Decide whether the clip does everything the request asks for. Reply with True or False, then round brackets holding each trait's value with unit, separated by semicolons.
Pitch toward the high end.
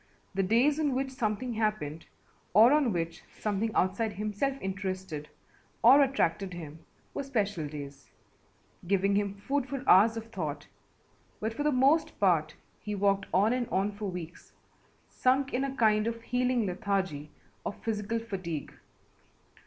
True (210 Hz)